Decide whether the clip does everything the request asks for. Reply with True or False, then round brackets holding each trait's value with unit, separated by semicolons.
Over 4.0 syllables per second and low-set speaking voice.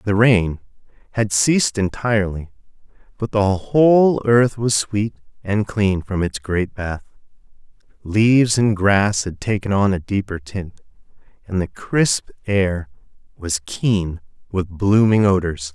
False (3.9 syllables/s; 100 Hz)